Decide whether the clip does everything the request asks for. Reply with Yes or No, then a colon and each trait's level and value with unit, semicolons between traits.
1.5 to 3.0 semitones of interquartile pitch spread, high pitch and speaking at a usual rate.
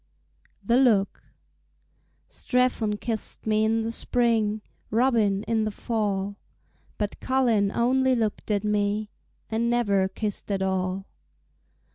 No: narrow, 2.6 semitones; high, 215 Hz; slow, 115 wpm